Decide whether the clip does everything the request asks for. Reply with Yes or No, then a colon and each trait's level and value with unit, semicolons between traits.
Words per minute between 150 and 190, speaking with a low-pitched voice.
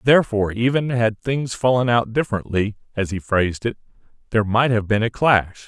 Yes: average, 180 wpm; low, 115 Hz